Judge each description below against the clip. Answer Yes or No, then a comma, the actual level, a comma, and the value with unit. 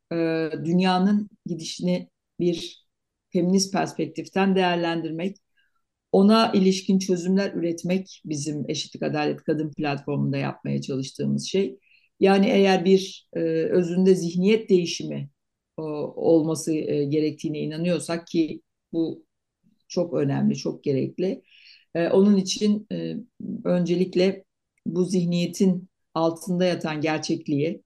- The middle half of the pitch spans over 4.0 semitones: No, average, 3.4 semitones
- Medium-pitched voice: Yes, medium, 170 Hz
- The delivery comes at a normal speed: No, slow, 90 wpm